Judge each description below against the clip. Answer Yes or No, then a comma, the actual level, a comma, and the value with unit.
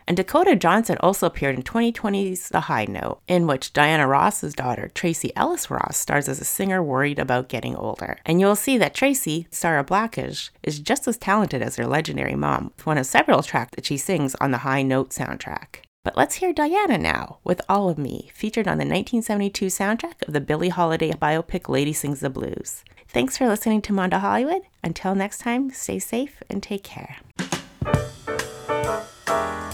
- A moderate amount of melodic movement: No, wide, 7.1 semitones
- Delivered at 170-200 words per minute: Yes, average, 185 wpm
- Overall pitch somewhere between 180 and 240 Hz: Yes, medium, 185 Hz